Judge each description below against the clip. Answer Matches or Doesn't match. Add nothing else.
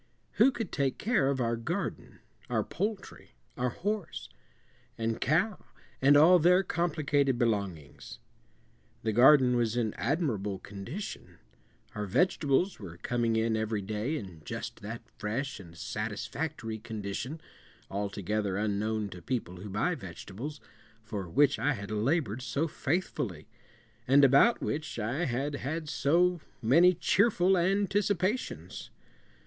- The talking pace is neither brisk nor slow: Doesn't match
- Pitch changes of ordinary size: Doesn't match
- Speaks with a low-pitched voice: Matches